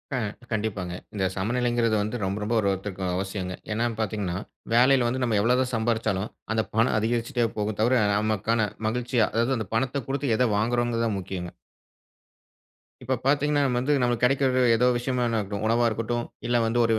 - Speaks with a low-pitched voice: Yes, low, 115 Hz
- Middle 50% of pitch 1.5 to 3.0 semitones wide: Yes, narrow, 2.6 semitones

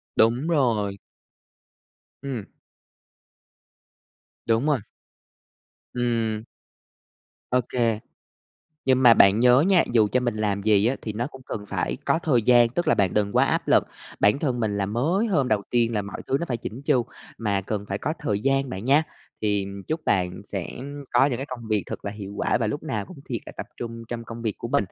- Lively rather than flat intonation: No, average, 4.0 semitones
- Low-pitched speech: Yes, low, 115 Hz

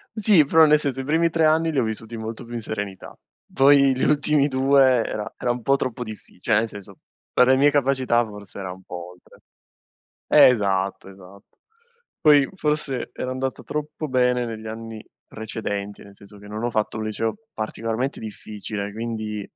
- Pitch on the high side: No, low, 115 Hz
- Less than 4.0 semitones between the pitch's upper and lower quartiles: No, average, 4.5 semitones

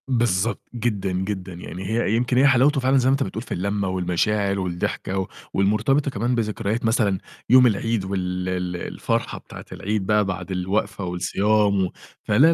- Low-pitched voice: Yes, low, 100 Hz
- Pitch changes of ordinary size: Yes, average, 3.9 semitones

